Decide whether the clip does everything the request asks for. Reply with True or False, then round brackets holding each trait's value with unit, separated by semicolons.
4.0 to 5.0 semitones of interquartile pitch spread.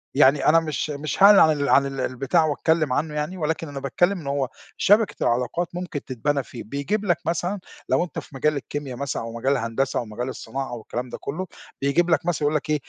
False (3.6 semitones)